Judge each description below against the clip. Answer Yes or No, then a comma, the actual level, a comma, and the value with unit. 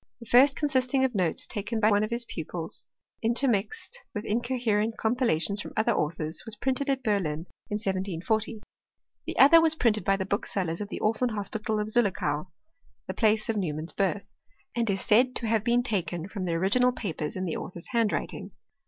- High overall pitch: Yes, high, 215 Hz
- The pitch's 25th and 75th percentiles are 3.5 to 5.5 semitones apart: Yes, average, 4.1 semitones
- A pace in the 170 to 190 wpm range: Yes, average, 185 wpm